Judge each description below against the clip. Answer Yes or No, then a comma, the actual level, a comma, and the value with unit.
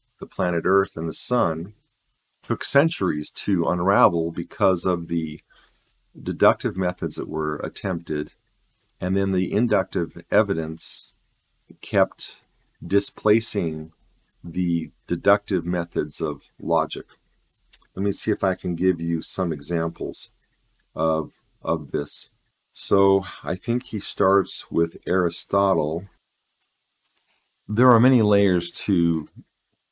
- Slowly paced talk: Yes, slow, 110 wpm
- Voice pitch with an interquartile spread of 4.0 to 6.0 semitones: No, average, 3.4 semitones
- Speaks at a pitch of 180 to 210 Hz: No, very low, 90 Hz